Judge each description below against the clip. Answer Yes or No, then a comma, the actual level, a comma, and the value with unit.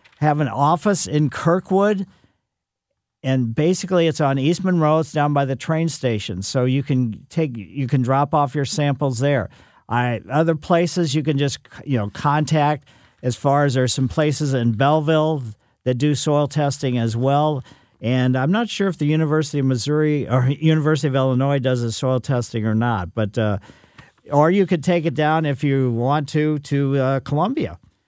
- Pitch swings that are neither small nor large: Yes, average, 3.4 semitones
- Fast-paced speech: No, average, 185 wpm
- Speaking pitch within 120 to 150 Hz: Yes, medium, 140 Hz